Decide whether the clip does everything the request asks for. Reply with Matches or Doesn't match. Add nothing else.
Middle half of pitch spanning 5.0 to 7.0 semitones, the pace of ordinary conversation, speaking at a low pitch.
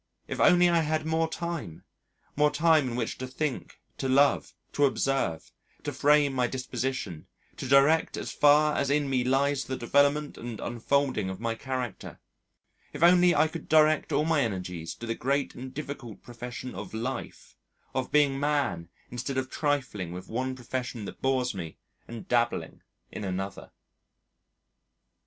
Doesn't match